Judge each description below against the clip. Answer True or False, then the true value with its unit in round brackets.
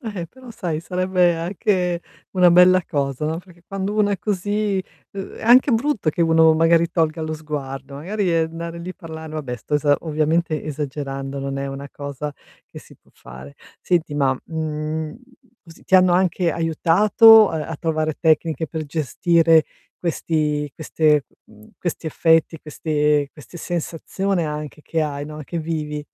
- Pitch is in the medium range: True (160 Hz)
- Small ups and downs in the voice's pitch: False (3.0 semitones)